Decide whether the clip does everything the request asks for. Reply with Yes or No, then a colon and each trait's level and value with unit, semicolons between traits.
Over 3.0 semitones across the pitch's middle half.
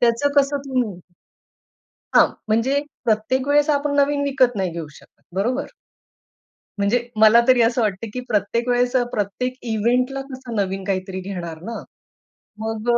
Yes: average, 4.0 semitones